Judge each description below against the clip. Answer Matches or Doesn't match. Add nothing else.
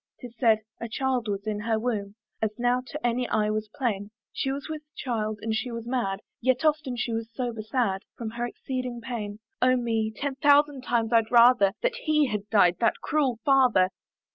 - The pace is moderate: Matches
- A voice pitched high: Matches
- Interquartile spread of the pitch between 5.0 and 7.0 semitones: Doesn't match